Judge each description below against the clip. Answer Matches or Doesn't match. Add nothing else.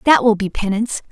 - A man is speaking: Doesn't match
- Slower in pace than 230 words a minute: Matches